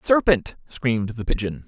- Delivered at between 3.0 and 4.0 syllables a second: No, 4.9 syllables/s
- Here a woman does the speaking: No, male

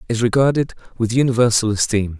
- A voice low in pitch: Yes, low, 115 Hz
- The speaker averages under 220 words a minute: Yes, slow, 135 wpm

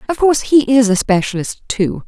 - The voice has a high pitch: Yes, high, 240 Hz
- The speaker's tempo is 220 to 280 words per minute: No, fast, 205 wpm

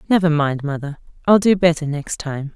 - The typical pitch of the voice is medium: Yes, medium, 160 Hz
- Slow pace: No, average, 190 wpm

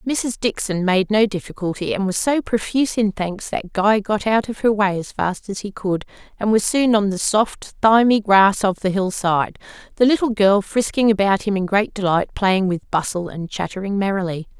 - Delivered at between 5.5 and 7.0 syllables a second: No, 4.9 syllables/s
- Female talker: Yes, female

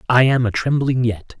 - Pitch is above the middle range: No, low, 125 Hz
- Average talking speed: Yes, average, 170 wpm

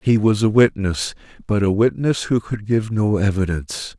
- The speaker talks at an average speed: Yes, average, 180 wpm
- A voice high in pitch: No, low, 105 Hz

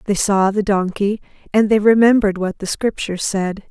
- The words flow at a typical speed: Yes, average, 180 wpm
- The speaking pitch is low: No, high, 205 Hz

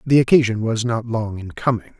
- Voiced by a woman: No, male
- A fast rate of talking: Yes, fast, 210 wpm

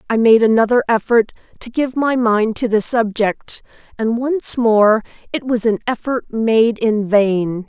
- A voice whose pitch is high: Yes, high, 230 Hz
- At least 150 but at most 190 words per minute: Yes, average, 155 wpm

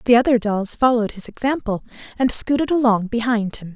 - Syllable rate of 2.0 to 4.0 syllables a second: No, 5.8 syllables/s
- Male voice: No, female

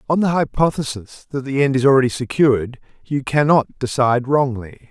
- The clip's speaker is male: Yes, male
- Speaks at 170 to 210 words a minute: No, average, 160 wpm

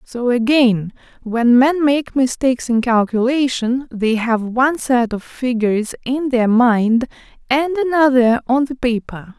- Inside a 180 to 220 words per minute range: No, average, 140 wpm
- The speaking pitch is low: No, very high, 250 Hz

